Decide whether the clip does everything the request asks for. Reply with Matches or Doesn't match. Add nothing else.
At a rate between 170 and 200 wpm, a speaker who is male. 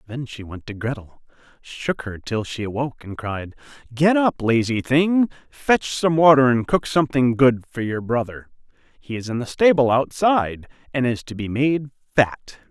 Matches